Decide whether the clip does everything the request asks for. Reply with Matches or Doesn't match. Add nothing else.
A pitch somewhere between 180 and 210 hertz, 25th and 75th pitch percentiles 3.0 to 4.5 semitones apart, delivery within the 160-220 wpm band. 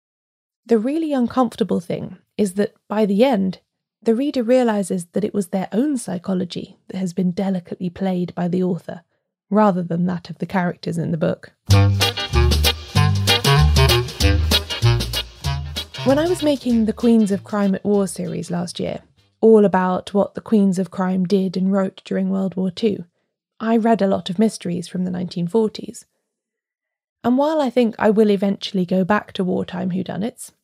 Matches